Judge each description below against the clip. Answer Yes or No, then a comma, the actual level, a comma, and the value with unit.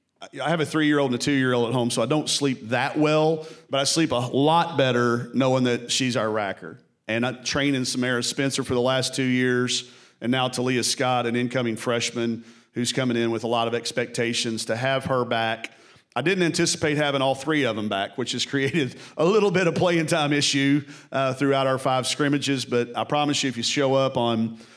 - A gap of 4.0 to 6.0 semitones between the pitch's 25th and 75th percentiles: No, average, 3.1 semitones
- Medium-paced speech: No, fast, 215 wpm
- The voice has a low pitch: Yes, low, 130 Hz